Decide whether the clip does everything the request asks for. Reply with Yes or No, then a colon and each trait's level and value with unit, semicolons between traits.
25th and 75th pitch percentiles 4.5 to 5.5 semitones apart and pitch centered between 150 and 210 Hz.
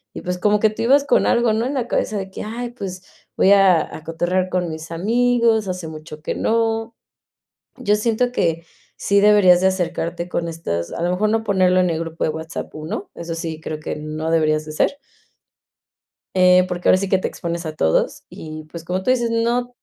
Yes: average, 4.9 semitones; medium, 185 Hz